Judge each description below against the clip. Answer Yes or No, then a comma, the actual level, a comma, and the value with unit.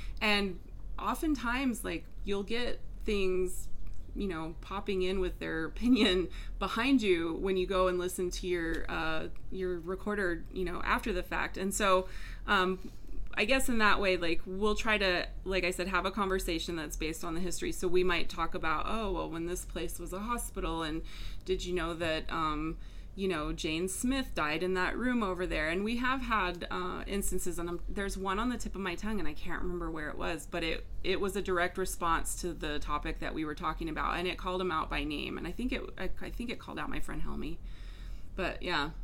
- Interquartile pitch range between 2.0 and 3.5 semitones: Yes, average, 2.9 semitones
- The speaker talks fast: Yes, fast, 220 wpm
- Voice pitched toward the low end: No, medium, 185 Hz